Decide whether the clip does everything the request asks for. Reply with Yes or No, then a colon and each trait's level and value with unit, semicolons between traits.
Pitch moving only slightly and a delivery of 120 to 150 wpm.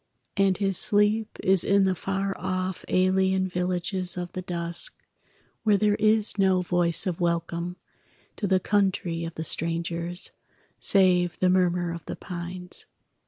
Yes: narrow, 1.9 semitones; average, 145 wpm